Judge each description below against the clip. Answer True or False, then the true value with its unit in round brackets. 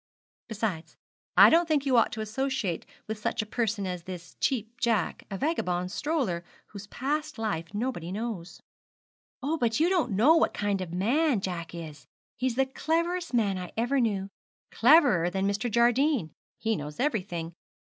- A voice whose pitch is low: False (220 Hz)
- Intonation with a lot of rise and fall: True (6.3 semitones)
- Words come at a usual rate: True (165 wpm)